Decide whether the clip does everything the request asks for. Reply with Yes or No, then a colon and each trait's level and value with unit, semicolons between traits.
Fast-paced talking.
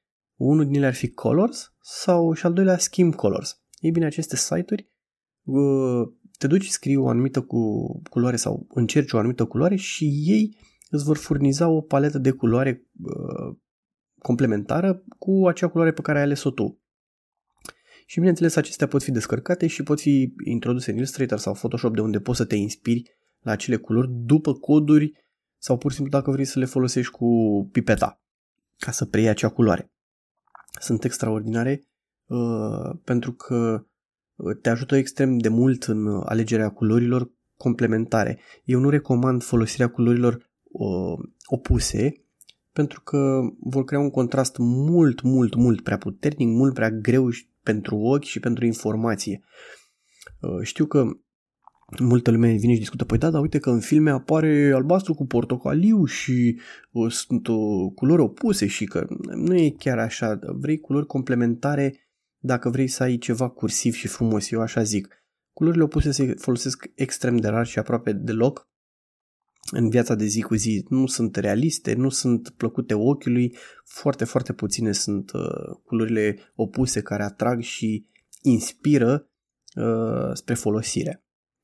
No: average, 150 wpm